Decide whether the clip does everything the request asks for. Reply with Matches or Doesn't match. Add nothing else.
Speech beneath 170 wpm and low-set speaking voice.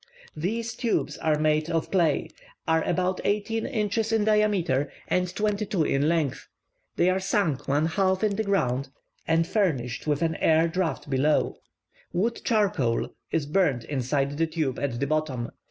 Doesn't match